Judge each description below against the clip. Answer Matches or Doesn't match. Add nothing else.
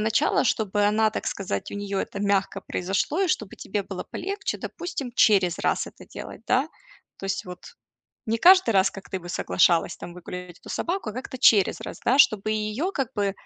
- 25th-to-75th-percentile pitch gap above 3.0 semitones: Matches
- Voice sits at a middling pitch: Doesn't match